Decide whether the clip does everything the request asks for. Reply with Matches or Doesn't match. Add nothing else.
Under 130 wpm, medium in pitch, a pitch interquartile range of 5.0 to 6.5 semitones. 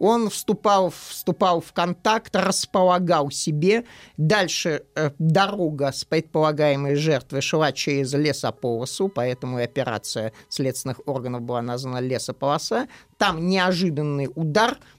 Matches